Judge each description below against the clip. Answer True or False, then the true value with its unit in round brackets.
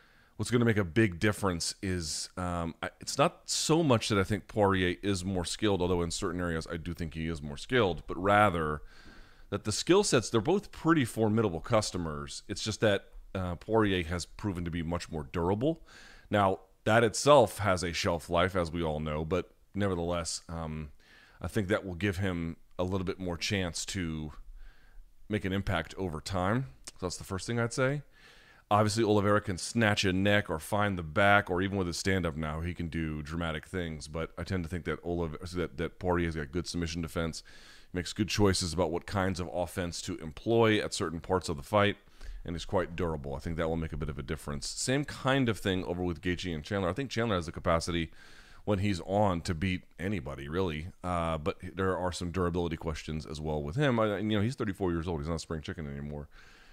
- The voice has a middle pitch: False (90 Hz)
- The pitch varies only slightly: False (3.7 semitones)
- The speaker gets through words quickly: True (215 wpm)